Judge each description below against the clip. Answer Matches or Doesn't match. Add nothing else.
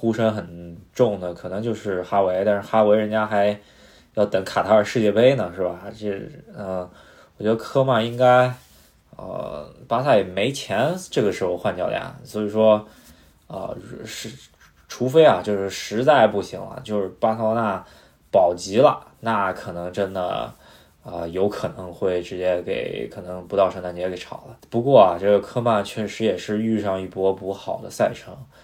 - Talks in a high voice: Doesn't match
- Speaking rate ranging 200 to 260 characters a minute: Matches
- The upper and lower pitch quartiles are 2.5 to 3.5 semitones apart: Matches